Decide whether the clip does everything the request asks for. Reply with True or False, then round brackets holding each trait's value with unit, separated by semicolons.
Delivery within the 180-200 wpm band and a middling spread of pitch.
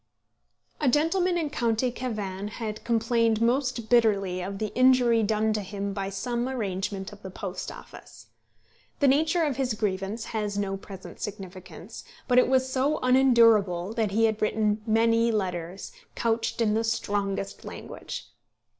False (150 wpm; 3.8 semitones)